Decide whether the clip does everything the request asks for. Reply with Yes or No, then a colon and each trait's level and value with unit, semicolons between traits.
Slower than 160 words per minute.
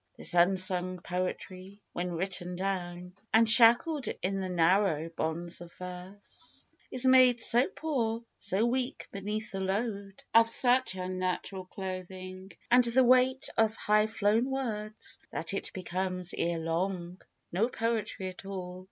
Yes: slow, 135 wpm